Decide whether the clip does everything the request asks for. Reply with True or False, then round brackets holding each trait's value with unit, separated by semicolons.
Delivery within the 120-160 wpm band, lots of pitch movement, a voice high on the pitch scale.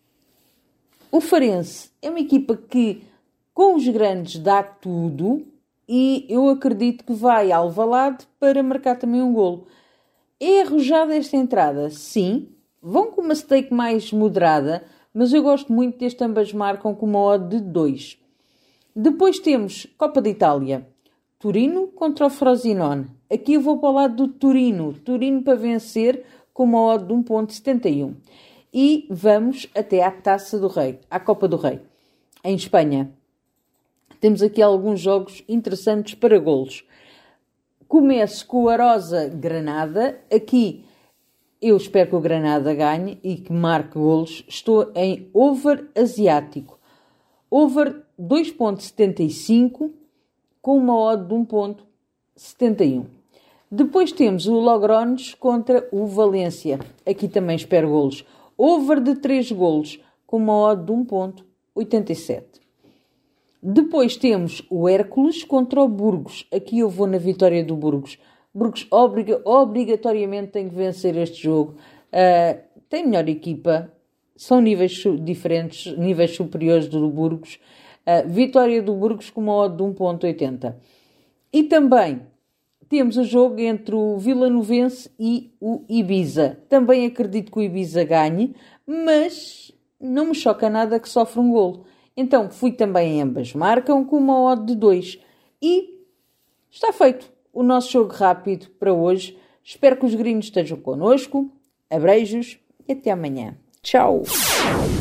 True (135 wpm; 6.0 semitones; 220 Hz)